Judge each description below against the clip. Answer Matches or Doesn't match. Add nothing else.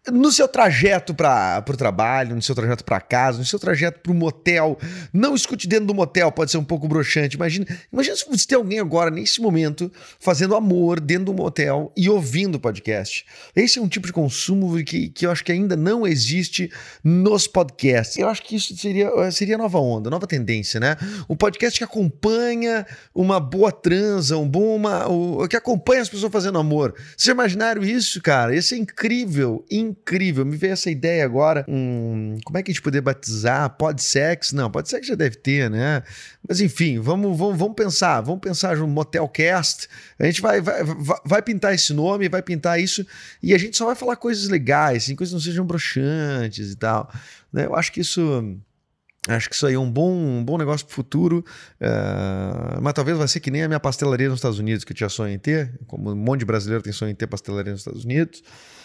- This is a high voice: Doesn't match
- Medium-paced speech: Doesn't match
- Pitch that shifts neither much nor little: Doesn't match